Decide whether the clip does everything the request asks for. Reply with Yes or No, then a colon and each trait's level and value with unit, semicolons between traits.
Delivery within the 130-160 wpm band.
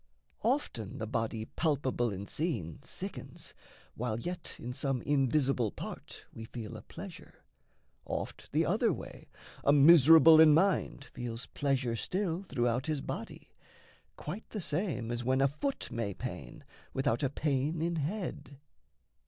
Yes: average, 140 wpm